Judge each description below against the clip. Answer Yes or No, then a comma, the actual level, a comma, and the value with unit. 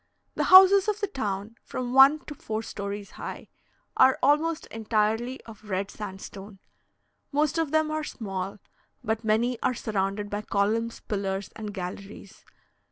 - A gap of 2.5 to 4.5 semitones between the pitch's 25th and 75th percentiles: No, average, 5.0 semitones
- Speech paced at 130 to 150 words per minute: Yes, average, 145 wpm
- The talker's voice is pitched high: Yes, high, 220 Hz